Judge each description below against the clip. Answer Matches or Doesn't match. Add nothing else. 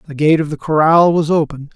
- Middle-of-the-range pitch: Matches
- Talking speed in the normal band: Doesn't match